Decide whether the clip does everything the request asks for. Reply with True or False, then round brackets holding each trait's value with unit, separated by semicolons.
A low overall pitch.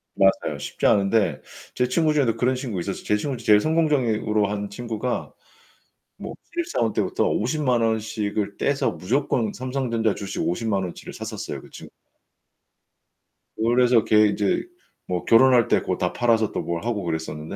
True (115 Hz)